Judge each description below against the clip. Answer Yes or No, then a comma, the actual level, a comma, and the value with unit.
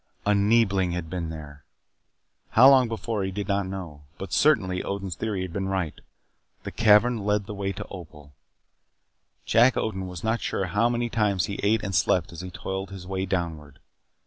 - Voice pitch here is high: No, very low, 95 Hz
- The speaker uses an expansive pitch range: No, average, 2.8 semitones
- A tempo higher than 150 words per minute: Yes, average, 185 wpm